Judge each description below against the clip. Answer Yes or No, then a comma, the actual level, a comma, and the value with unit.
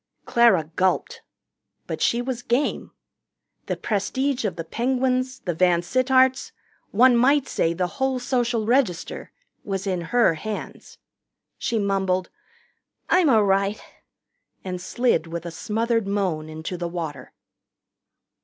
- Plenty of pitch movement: Yes, wide, 5.9 semitones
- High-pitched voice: Yes, high, 210 Hz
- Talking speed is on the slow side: Yes, slow, 125 wpm